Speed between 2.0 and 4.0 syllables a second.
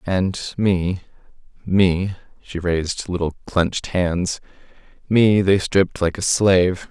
Yes: 3.8 syllables/s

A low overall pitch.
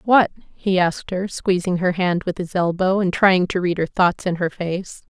No: medium, 185 Hz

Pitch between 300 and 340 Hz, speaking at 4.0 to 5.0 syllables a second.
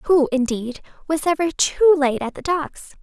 Yes: very high, 305 Hz; 4.6 syllables/s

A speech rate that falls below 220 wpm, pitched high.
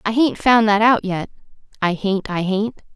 Yes: fast, 205 wpm; high, 205 Hz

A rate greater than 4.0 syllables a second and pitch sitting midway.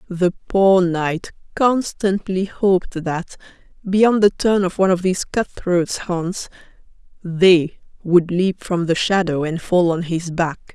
No: 3.8 syllables/s; medium, 180 Hz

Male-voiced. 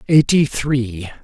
Yes: male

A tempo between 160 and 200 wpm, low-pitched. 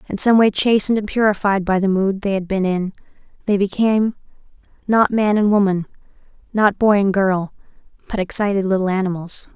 No: average, 170 wpm; high, 200 Hz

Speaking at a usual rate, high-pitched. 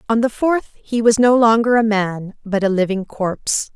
No: fast, 210 wpm; high, 220 Hz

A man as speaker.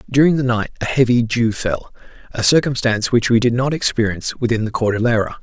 Yes: male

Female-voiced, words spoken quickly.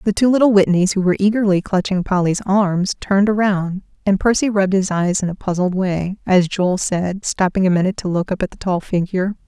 Yes: female; fast, 215 wpm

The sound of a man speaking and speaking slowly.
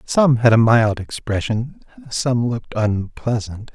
Yes: male; slow, 130 wpm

